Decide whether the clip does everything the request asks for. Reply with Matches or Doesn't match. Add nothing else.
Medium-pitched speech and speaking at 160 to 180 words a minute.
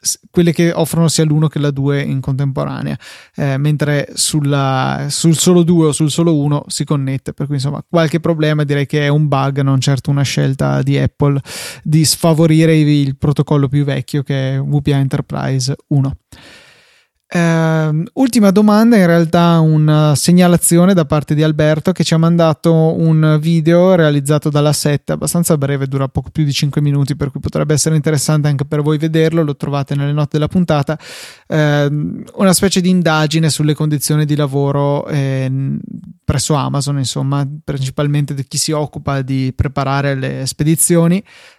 Matches